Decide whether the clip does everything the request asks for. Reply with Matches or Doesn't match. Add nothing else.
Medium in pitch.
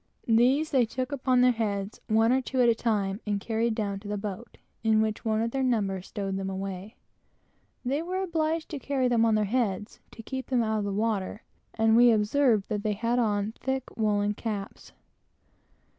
Doesn't match